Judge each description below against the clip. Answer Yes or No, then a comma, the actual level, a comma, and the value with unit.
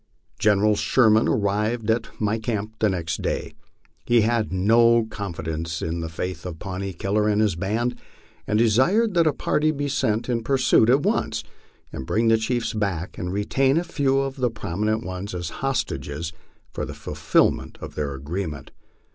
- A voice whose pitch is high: No, low, 105 Hz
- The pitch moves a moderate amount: Yes, average, 4.6 semitones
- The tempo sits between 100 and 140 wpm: No, average, 165 wpm